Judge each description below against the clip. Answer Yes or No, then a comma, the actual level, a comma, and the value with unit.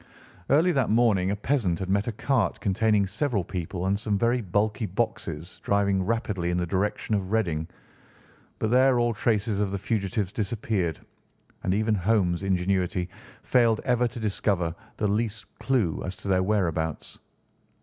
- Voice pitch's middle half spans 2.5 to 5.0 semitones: Yes, average, 3.5 semitones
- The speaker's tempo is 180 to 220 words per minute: No, average, 160 wpm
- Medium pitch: No, low, 100 Hz